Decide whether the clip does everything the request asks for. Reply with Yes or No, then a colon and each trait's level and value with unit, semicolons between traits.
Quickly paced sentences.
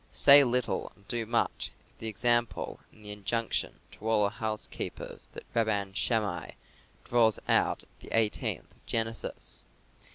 No: average, 150 wpm